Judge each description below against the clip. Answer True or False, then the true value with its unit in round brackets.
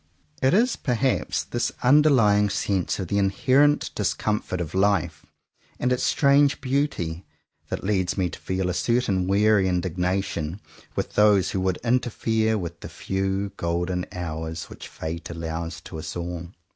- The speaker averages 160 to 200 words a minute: False (145 wpm)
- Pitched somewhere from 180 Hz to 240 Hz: False (95 Hz)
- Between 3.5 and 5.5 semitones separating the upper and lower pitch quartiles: True (5.0 semitones)